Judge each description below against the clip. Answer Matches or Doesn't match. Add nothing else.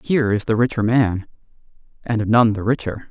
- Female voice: Doesn't match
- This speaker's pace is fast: Doesn't match